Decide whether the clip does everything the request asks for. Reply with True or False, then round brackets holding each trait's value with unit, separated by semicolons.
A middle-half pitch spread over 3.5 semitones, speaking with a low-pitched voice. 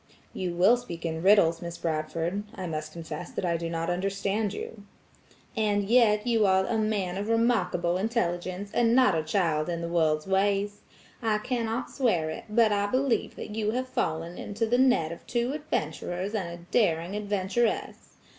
False (4.6 semitones; 195 Hz)